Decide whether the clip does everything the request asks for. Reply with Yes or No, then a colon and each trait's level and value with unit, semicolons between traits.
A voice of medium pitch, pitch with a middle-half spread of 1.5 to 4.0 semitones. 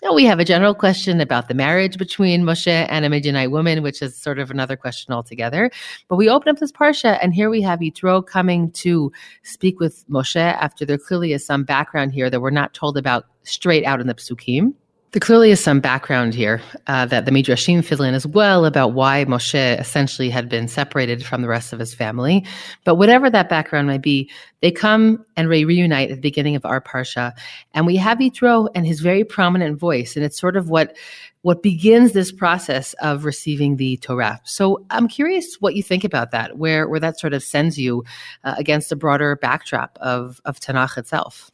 No: medium, 150 Hz; wide, 5.6 semitones